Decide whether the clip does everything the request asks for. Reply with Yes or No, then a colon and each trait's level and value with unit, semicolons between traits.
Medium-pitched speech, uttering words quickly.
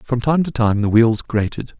No: low, 120 Hz; fast, 235 wpm